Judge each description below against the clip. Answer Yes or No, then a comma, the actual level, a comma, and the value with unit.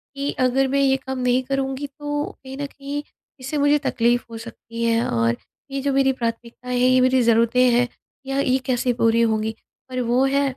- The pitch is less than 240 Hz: No, very high, 255 Hz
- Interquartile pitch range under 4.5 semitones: Yes, narrow, 2.5 semitones